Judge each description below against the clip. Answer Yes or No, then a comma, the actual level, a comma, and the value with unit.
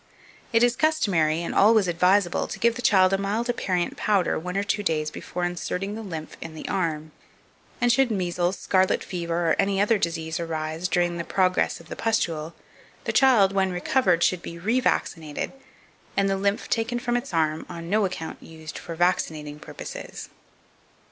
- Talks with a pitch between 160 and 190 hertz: Yes, medium, 185 Hz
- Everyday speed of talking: Yes, average, 180 wpm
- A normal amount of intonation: Yes, average, 3.7 semitones